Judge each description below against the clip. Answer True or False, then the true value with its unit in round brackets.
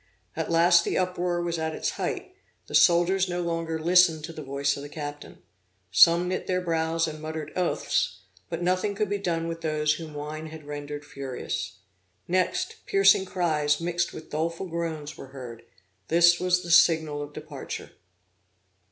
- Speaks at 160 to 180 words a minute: True (170 wpm)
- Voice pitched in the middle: True (165 Hz)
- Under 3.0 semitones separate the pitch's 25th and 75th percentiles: True (2.6 semitones)